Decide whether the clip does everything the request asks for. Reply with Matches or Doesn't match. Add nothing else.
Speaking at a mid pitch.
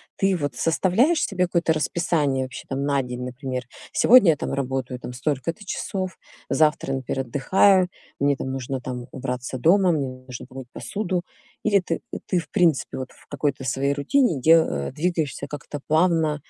Matches